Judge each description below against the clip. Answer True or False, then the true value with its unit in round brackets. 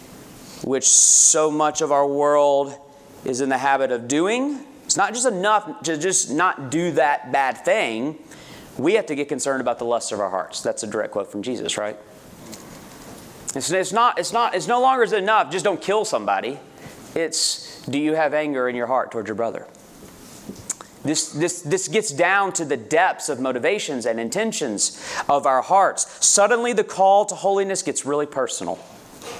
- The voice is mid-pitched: True (155 Hz)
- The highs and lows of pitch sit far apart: True (6.3 semitones)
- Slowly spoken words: False (180 wpm)